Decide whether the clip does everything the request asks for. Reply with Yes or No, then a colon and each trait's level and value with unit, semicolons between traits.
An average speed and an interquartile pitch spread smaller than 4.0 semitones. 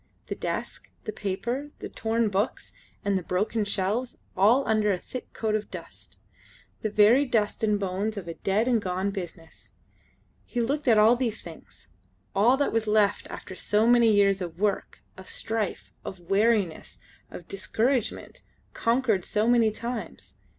Yes: average, 160 wpm; average, 2.9 semitones